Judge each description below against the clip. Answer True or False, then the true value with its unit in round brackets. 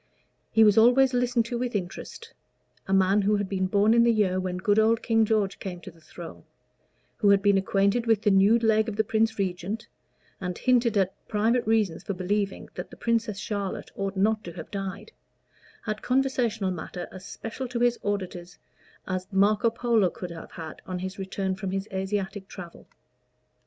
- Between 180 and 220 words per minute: True (190 wpm)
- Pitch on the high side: True (205 Hz)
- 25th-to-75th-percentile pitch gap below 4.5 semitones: True (2.9 semitones)